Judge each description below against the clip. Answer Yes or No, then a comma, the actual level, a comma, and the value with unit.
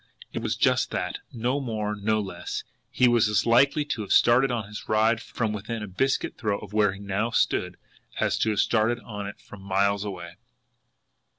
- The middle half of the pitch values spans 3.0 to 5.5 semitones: No, narrow, 2.6 semitones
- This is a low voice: Yes, low, 110 Hz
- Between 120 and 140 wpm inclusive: No, average, 195 wpm